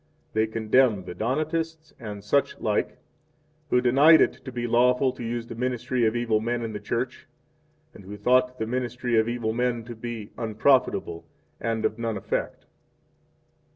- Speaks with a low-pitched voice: Yes, low, 120 Hz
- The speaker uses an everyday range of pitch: No, narrow, 2.3 semitones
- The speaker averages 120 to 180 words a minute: Yes, average, 170 wpm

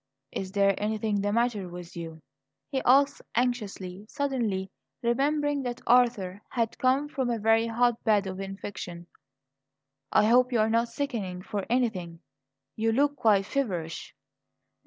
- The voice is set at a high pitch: Yes, high, 225 Hz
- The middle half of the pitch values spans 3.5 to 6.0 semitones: Yes, average, 4.2 semitones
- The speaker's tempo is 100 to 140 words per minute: Yes, slow, 135 wpm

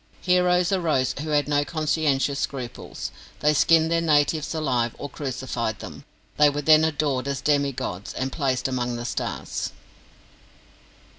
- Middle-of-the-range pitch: Yes, medium, 145 Hz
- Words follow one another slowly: No, average, 145 wpm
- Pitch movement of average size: Yes, average, 3.3 semitones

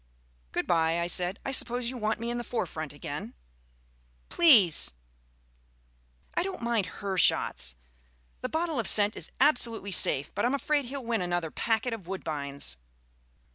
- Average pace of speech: Yes, average, 155 wpm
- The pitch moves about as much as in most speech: No, wide, 6.6 semitones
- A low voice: No, high, 215 Hz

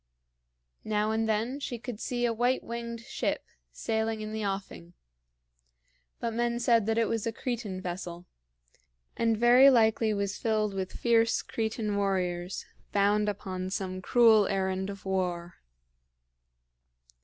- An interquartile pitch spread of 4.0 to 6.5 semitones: No, average, 3.1 semitones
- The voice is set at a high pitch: Yes, high, 215 Hz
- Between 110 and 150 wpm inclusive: Yes, slow, 135 wpm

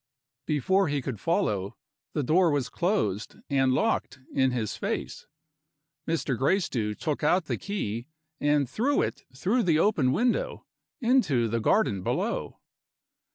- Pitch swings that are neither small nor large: No, wide, 7.5 semitones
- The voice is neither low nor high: Yes, medium, 145 Hz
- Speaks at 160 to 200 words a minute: No, slow, 135 wpm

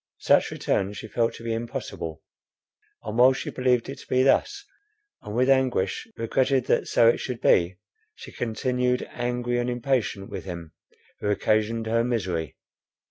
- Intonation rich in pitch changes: No, average, 3.1 semitones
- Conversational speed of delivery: Yes, average, 160 wpm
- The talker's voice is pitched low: Yes, low, 115 Hz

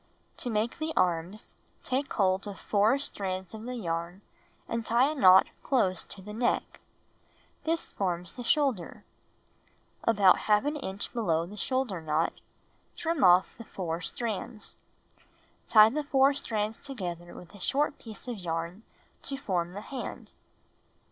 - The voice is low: No, high, 210 Hz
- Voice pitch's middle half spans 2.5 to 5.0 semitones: No, wide, 5.6 semitones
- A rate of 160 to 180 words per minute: No, average, 145 wpm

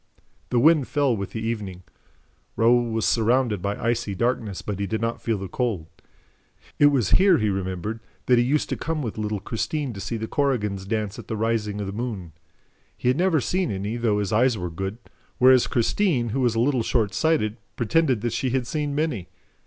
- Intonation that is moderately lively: Yes, average, 3.9 semitones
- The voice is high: No, low, 115 Hz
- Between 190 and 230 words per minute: Yes, average, 200 wpm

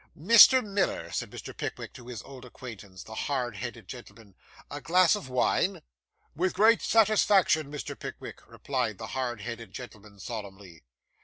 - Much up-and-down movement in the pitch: Yes, wide, 8.8 semitones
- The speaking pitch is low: Yes, low, 125 Hz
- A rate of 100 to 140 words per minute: No, average, 150 wpm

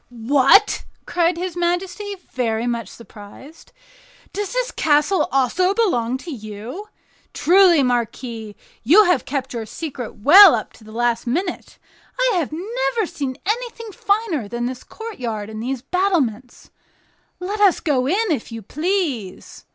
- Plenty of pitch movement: Yes, wide, 8.1 semitones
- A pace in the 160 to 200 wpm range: No, average, 140 wpm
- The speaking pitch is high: Yes, very high, 290 Hz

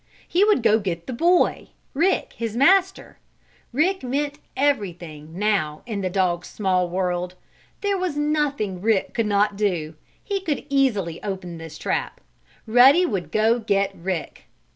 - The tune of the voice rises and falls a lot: Yes, wide, 7.8 semitones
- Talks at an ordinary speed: Yes, average, 145 wpm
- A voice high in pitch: Yes, high, 215 Hz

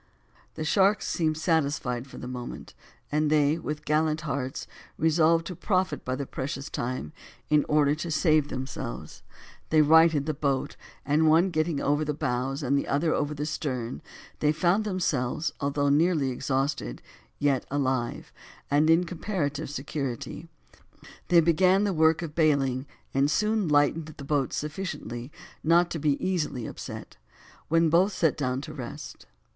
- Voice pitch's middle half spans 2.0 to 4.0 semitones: Yes, average, 2.9 semitones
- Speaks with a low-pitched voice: No, medium, 150 Hz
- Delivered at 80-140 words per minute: No, average, 150 wpm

